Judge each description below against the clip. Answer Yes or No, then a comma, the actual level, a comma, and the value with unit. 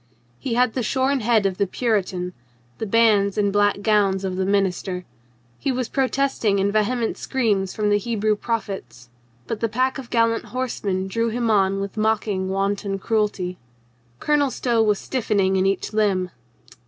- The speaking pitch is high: Yes, high, 210 Hz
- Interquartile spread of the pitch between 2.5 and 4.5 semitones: Yes, average, 3.0 semitones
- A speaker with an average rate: Yes, average, 165 wpm